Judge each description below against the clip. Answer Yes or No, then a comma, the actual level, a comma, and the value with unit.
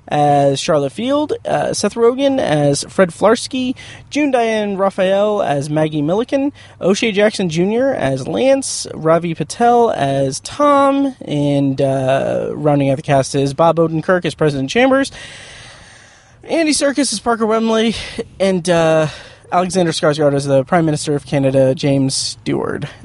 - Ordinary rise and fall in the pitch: No, wide, 8.4 semitones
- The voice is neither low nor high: Yes, medium, 170 Hz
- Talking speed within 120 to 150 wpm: Yes, average, 140 wpm